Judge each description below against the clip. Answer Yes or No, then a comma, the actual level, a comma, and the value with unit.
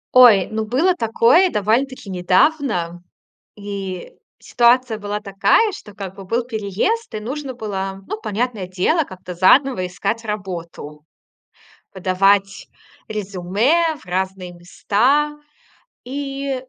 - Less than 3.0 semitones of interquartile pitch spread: No, average, 5.2 semitones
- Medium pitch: No, high, 210 Hz